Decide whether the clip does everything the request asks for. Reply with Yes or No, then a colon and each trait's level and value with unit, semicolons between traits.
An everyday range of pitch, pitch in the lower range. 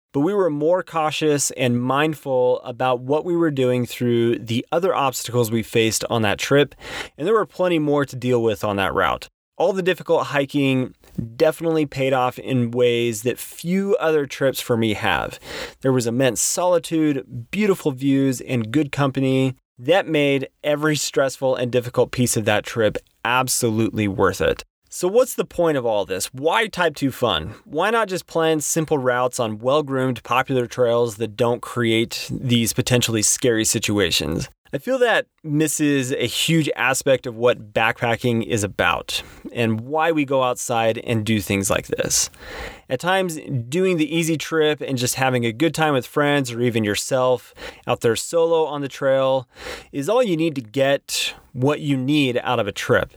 Yes: average, 4.2 semitones; low, 130 Hz